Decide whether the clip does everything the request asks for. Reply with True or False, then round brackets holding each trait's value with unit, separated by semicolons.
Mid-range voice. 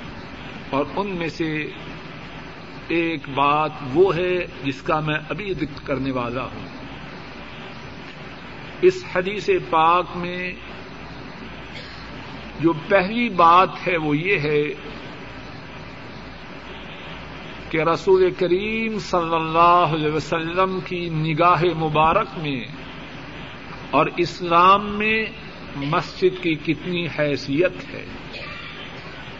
True (170 Hz)